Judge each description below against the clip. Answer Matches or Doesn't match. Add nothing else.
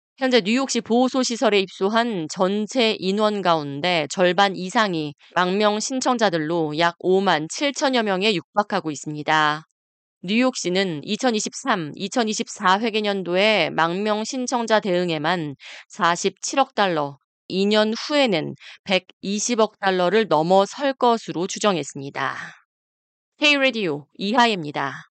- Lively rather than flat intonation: Doesn't match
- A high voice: Matches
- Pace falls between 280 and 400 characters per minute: Doesn't match